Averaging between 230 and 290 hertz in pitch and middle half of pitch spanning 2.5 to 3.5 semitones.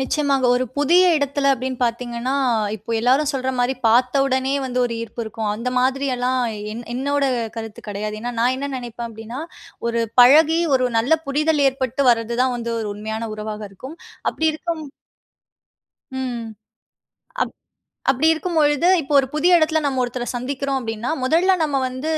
Yes: very high, 255 Hz; average, 3.2 semitones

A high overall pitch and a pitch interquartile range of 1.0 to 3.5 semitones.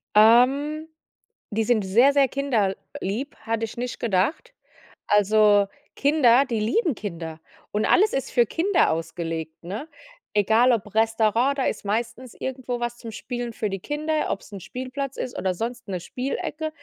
No: high, 235 Hz; average, 4.6 semitones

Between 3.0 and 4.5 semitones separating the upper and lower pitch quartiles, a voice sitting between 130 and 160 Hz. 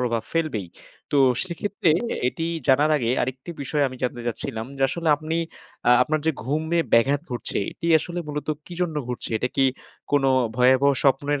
Yes: average, 3.9 semitones; medium, 140 Hz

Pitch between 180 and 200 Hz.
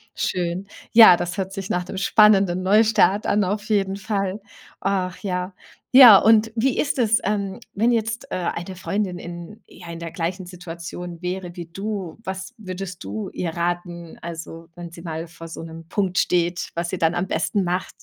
Yes: medium, 185 Hz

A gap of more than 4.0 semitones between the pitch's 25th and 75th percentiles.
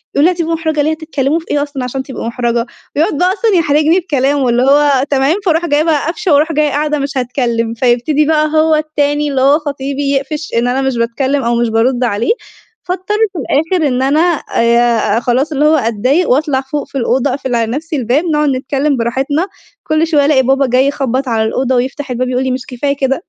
No: average, 3.3 semitones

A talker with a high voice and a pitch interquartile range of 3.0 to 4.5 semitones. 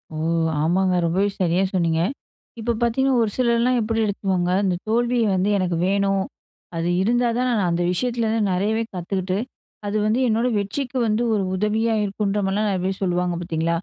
Yes: high, 200 Hz; average, 3.8 semitones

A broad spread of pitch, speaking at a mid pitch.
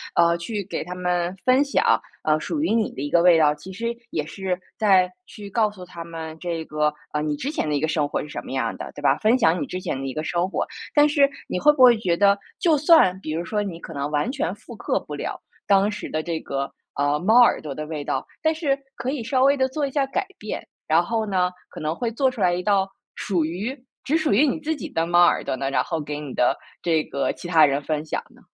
Yes: wide, 7.3 semitones; medium, 180 Hz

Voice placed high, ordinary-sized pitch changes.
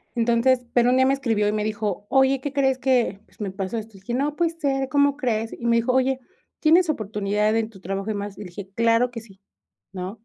Yes: high, 230 Hz; average, 4.2 semitones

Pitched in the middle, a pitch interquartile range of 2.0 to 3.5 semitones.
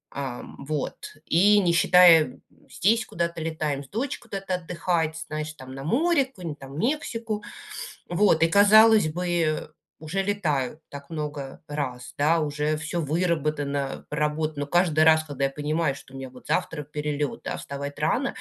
No: medium, 155 Hz; average, 3.9 semitones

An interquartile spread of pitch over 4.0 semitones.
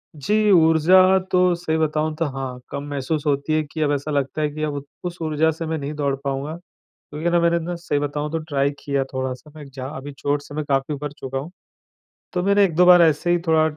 No: average, 2.8 semitones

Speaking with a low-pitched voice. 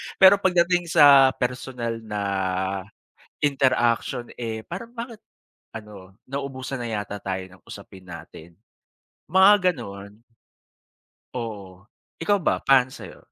Yes: low, 125 Hz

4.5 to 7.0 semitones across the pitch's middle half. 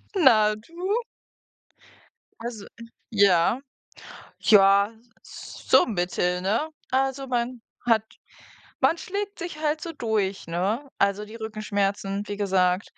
Yes: average, 5.2 semitones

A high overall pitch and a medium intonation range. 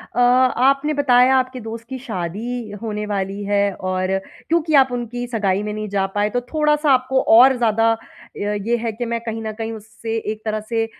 Yes: high, 230 Hz; average, 3.3 semitones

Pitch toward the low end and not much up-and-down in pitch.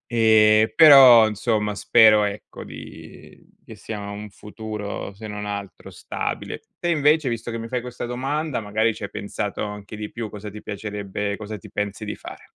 Yes: low, 105 Hz; narrow, 2.0 semitones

